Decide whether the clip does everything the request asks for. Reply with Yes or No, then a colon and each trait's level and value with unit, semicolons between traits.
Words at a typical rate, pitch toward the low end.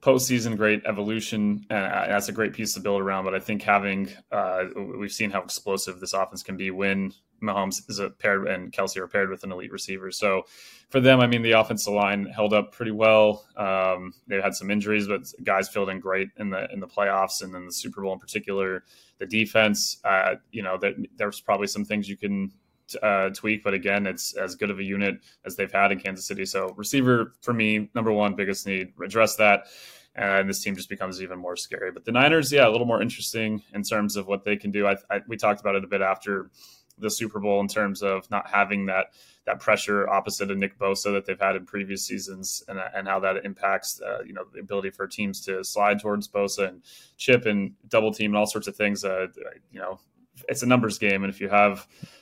No: fast, 230 wpm; low, 100 Hz